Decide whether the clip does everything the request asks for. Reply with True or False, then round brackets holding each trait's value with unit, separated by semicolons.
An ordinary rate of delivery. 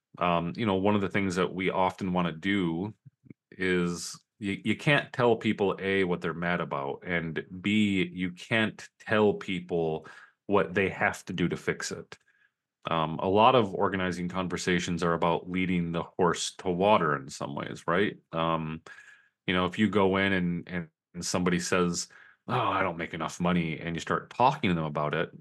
True (190 wpm)